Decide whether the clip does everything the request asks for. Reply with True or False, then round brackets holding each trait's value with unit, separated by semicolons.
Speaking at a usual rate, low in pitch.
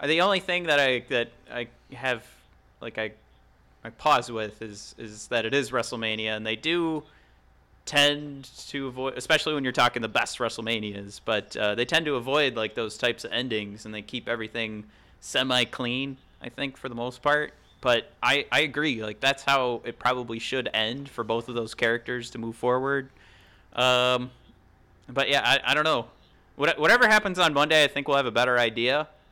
True (190 wpm; 125 Hz)